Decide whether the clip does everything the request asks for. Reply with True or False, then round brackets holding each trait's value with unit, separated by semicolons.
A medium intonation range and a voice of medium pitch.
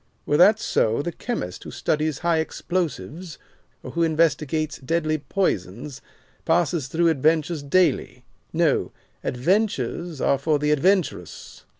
True (3.3 semitones; 155 Hz)